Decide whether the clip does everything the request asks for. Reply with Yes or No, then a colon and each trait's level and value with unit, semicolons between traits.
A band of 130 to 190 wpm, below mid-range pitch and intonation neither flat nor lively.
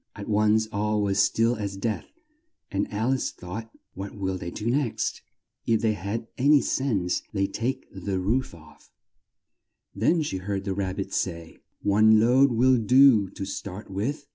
Yes: average, 170 wpm; low, 105 Hz; average, 3.3 semitones